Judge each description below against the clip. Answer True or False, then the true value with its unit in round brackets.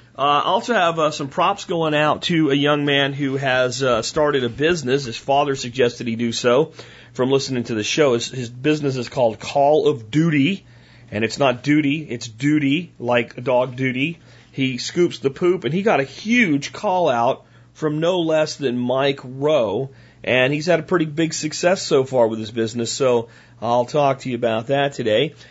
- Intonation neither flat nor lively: True (3.8 semitones)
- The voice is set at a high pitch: False (135 Hz)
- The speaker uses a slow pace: False (200 wpm)